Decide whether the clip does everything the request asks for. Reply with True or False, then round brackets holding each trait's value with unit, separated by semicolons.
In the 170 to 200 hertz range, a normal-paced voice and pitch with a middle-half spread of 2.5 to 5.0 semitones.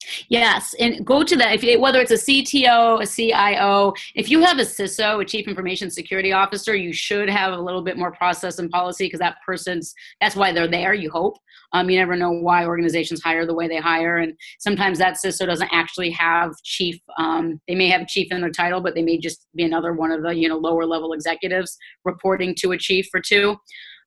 False (185 Hz; 220 wpm; 3.0 semitones)